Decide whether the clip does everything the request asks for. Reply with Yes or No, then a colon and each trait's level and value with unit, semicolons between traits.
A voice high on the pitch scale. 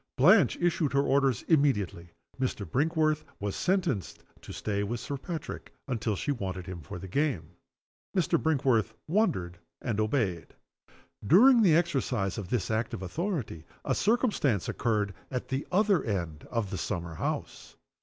No: low, 125 Hz